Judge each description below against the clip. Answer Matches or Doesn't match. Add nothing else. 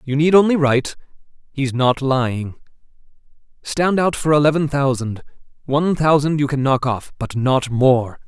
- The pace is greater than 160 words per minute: Doesn't match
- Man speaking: Matches